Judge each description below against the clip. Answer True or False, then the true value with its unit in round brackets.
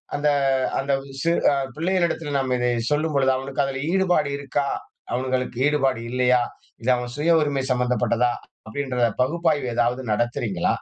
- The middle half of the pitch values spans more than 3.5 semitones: False (3.2 semitones)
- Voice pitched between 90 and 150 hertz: True (135 Hz)